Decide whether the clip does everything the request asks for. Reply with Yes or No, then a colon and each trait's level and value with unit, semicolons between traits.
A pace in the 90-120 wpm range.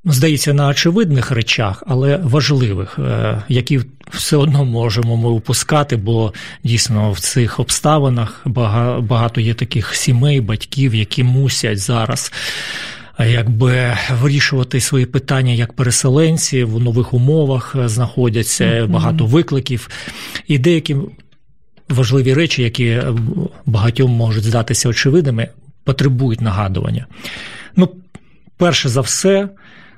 Yes: slow, 105 wpm